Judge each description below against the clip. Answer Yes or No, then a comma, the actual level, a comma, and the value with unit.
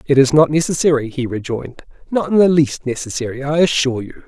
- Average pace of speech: Yes, average, 195 wpm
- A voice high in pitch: No, medium, 140 Hz